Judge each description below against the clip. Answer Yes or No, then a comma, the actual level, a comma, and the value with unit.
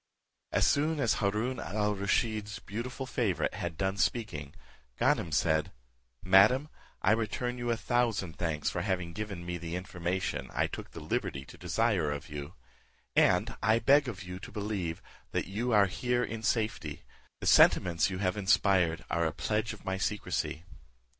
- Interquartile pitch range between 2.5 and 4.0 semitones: No, average, 4.5 semitones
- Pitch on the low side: Yes, low, 100 Hz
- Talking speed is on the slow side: No, average, 165 wpm